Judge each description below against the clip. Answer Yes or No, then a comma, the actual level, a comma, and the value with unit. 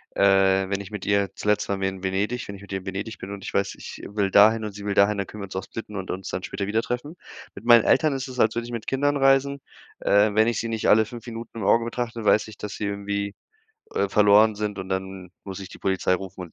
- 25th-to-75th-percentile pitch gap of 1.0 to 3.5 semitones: Yes, average, 2.7 semitones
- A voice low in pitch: Yes, low, 105 Hz